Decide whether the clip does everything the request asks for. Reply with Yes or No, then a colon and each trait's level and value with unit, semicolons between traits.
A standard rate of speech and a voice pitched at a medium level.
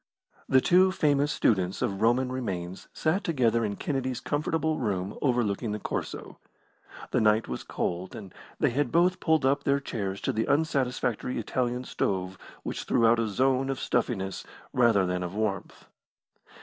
No: average, 160 wpm; low, 120 Hz